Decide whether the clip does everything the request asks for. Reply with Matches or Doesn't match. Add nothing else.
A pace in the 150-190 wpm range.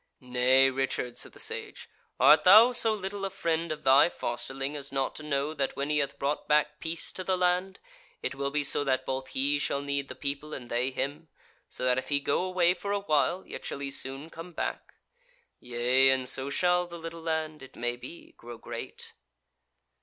Doesn't match